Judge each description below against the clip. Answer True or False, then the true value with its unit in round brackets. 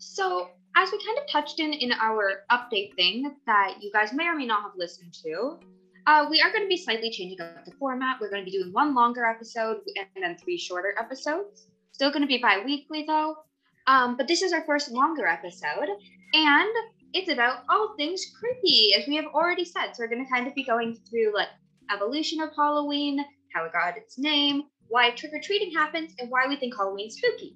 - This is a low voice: False (260 Hz)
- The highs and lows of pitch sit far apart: True (7.1 semitones)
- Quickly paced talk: True (210 wpm)